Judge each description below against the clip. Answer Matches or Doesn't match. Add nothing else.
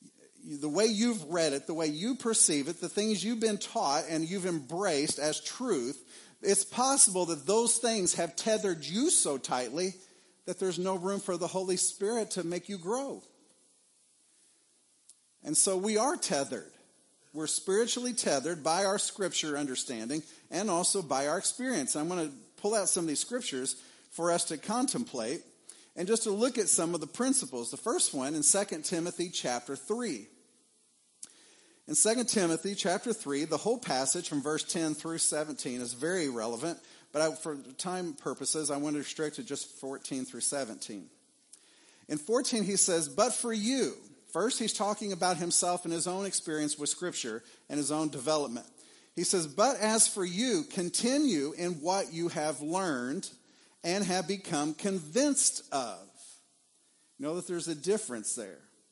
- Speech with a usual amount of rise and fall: Doesn't match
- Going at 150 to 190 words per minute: Matches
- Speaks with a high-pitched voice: Doesn't match